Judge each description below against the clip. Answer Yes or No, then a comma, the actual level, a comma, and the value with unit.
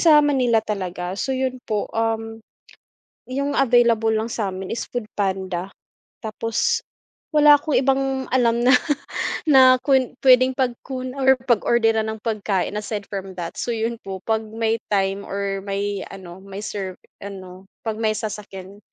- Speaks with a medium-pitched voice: No, high, 220 Hz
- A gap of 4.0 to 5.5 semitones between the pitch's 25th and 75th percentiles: Yes, average, 4.3 semitones